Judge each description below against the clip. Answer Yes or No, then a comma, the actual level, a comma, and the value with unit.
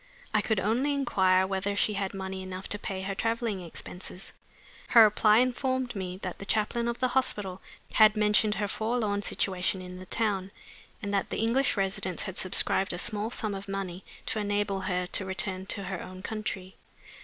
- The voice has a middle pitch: No, high, 200 Hz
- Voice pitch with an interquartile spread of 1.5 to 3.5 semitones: Yes, narrow, 2.5 semitones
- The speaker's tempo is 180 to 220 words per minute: Yes, average, 185 wpm